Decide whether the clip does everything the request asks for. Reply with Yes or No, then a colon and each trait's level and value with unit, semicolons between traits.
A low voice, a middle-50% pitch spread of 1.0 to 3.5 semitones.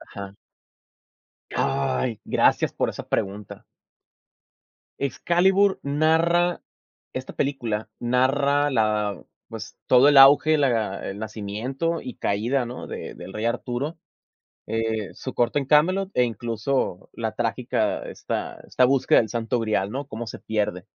No: low, 120 Hz; average, 4.6 semitones